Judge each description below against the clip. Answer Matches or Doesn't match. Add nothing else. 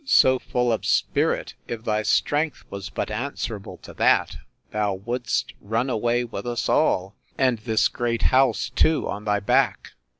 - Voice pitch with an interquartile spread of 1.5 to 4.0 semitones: Matches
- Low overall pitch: Matches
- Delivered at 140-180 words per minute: Matches